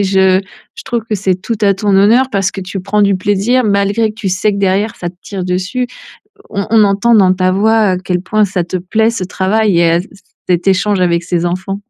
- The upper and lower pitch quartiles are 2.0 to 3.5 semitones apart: Yes, narrow, 2.4 semitones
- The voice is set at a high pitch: Yes, high, 195 Hz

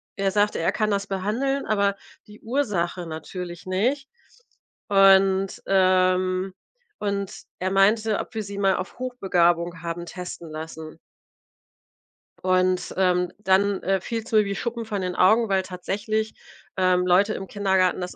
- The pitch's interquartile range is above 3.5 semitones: No, narrow, 2.4 semitones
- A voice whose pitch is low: No, high, 195 Hz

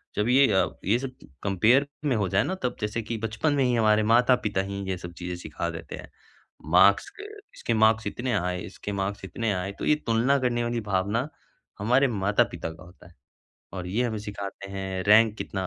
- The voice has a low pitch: Yes, low, 105 Hz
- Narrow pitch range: No, average, 3.6 semitones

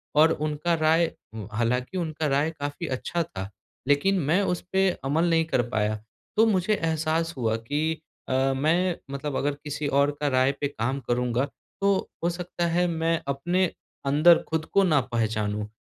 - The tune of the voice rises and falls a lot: No, average, 4.4 semitones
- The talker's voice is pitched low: No, medium, 150 Hz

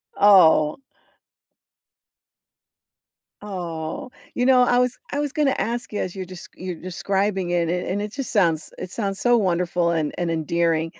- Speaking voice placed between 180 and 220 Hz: Yes, medium, 185 Hz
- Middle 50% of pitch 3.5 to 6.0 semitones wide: Yes, average, 4.2 semitones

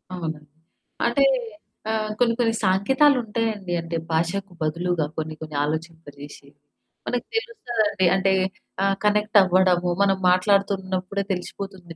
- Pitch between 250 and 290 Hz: No, high, 190 Hz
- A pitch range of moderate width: Yes, average, 3.6 semitones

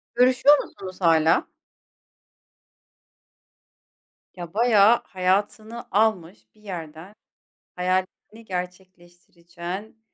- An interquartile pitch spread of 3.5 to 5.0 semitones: Yes, average, 3.8 semitones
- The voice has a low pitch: No, medium, 185 Hz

